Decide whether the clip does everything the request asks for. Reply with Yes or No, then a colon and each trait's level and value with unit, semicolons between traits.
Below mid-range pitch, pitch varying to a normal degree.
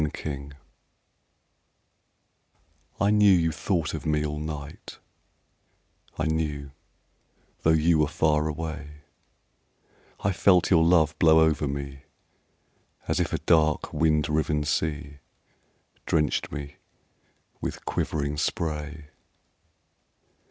No: very low, 75 Hz; narrow, 1.5 semitones